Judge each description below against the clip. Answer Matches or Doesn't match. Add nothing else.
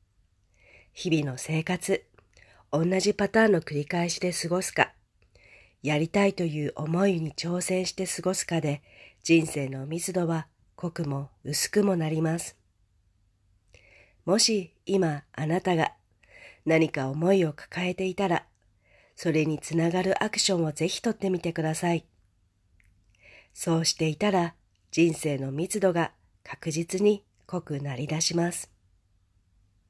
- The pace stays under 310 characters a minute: Matches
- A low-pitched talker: Doesn't match